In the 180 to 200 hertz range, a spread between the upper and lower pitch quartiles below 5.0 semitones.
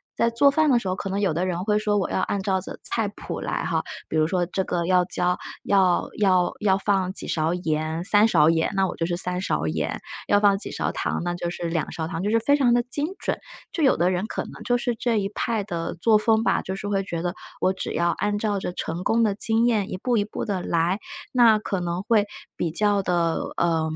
Yes: high, 190 Hz; average, 3.6 semitones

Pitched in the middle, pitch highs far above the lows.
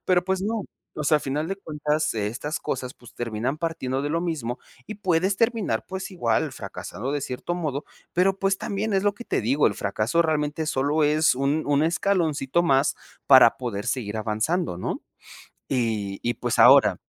Yes: medium, 150 Hz; wide, 5.9 semitones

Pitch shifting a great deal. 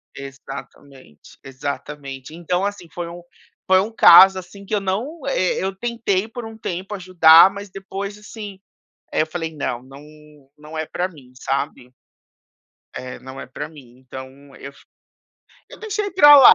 Yes: wide, 6.4 semitones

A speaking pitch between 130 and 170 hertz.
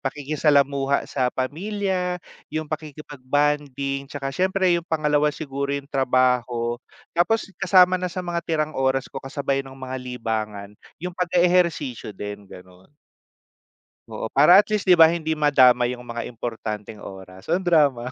Yes: medium, 140 Hz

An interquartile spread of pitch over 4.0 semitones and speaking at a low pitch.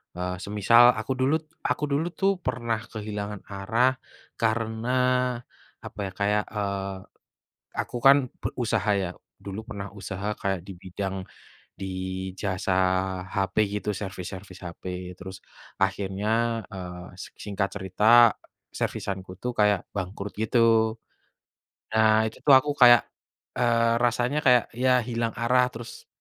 No: average, 3.5 semitones; low, 105 Hz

